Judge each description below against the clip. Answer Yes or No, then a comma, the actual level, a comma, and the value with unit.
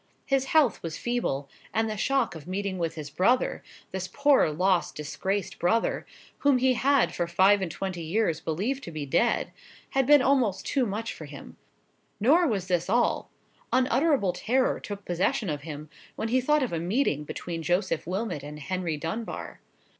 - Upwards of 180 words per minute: No, average, 165 wpm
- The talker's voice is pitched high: Yes, high, 195 Hz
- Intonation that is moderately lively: No, wide, 7.1 semitones